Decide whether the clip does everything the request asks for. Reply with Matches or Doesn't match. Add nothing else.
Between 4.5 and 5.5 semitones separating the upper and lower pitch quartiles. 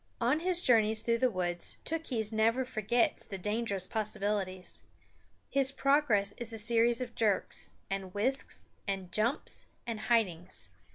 Doesn't match